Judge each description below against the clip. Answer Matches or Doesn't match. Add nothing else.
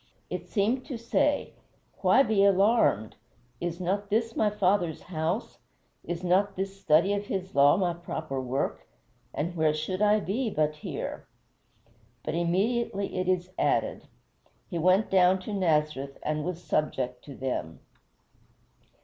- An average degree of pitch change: Matches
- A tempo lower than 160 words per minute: Matches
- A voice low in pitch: Doesn't match